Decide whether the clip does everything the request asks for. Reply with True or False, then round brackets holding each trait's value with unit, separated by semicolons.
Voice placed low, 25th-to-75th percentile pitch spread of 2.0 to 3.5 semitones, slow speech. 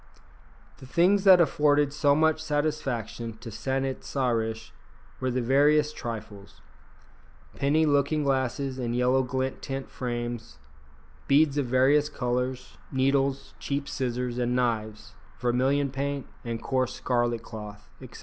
True (130 Hz; 3.0 semitones; 130 wpm)